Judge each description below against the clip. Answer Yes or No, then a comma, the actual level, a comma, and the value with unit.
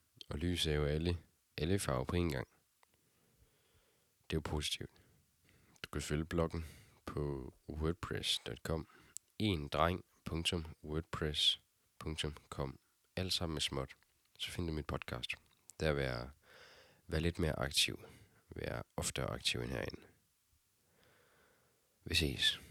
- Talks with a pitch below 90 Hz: Yes, very low, 80 Hz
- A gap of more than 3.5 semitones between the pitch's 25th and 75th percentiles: No, average, 3.0 semitones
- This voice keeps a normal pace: No, slow, 115 wpm